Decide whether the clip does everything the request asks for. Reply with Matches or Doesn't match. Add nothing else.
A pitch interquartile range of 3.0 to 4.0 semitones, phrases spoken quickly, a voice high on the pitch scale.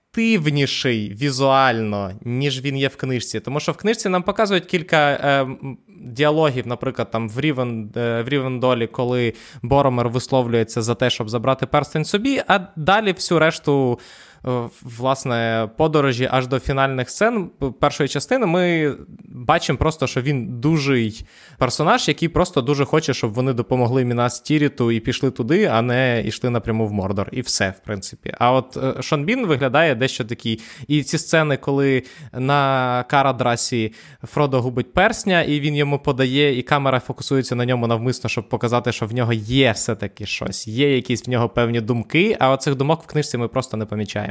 Doesn't match